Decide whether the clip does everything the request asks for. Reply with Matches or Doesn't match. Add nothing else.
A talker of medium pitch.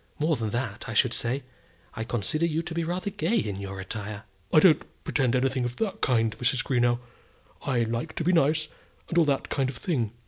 Doesn't match